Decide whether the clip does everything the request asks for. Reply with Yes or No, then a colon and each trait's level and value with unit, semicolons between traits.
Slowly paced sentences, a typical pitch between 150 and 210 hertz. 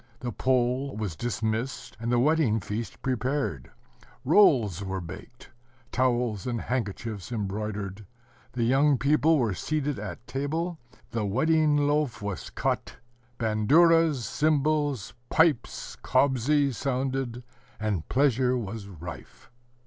No: slow, 110 wpm; low, 125 Hz